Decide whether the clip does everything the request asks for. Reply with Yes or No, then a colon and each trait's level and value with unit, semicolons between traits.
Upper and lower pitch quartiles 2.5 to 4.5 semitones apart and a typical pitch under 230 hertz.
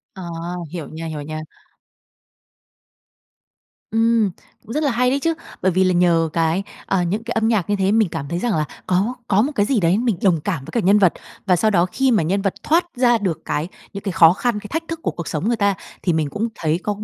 No: average, 5.1 semitones; high, 195 Hz